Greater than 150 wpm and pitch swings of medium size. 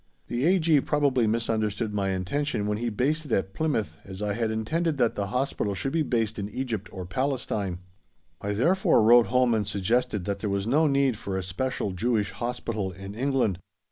Yes: average, 190 wpm; average, 4.6 semitones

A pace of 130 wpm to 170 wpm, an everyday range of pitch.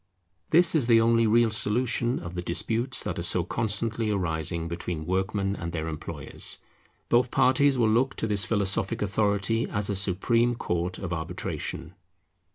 Yes: average, 160 wpm; average, 4.5 semitones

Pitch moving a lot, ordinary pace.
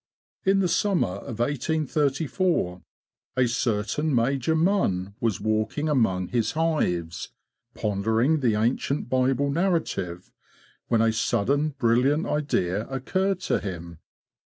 No: wide, 6.4 semitones; slow, 110 wpm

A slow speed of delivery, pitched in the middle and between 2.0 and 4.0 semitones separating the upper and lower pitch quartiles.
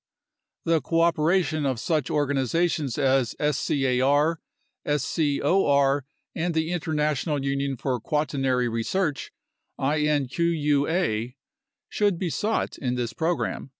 Yes: slow, 95 wpm; medium, 145 Hz; average, 3.3 semitones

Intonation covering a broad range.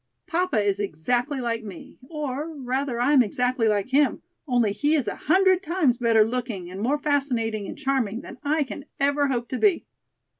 No: average, 4.3 semitones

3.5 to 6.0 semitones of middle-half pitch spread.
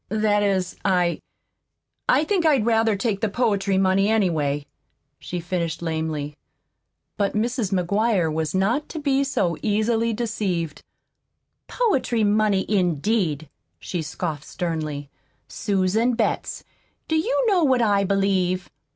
Yes: average, 4.5 semitones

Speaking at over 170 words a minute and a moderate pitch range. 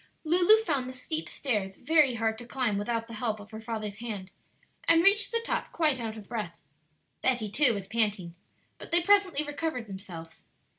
No: average, 185 wpm; wide, 6.5 semitones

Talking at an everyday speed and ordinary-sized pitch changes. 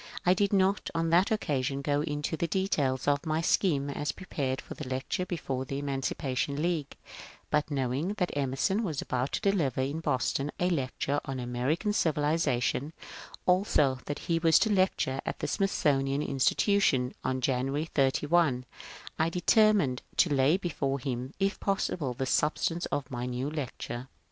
Yes: average, 165 wpm; average, 4.6 semitones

